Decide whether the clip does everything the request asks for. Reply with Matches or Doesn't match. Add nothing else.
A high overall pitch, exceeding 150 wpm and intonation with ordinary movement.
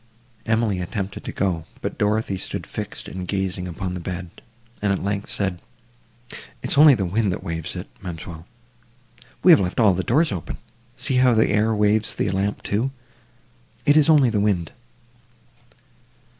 Doesn't match